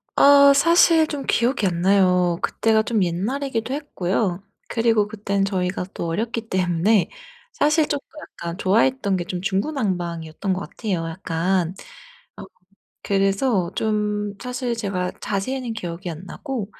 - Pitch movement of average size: Yes, average, 4.8 semitones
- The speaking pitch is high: Yes, high, 200 Hz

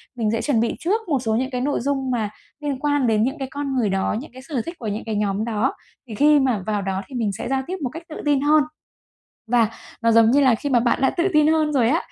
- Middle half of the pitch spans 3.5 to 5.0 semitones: Yes, average, 4.4 semitones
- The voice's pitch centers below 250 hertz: No, very high, 255 Hz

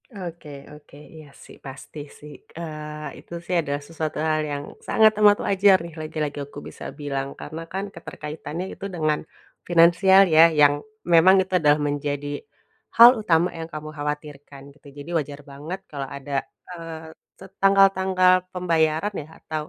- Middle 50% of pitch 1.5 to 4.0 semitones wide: Yes, average, 3.6 semitones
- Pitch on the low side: No, medium, 155 Hz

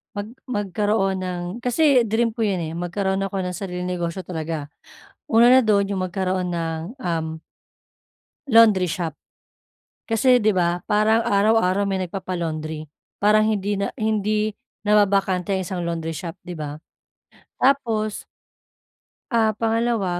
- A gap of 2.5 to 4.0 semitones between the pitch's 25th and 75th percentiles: Yes, average, 3.4 semitones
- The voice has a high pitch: Yes, high, 195 Hz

